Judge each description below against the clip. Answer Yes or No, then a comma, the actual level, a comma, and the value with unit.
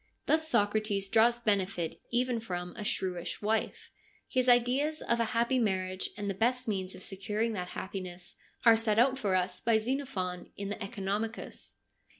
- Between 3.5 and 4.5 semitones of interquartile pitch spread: Yes, average, 3.8 semitones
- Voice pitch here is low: No, high, 215 Hz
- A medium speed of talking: Yes, average, 160 wpm